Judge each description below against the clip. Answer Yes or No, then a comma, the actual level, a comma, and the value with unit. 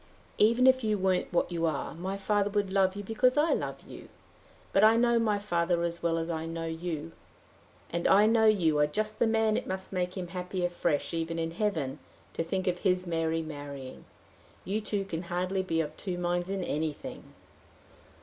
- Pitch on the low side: No, medium, 180 Hz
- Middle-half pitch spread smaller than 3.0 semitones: No, average, 3.8 semitones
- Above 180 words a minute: Yes, average, 200 wpm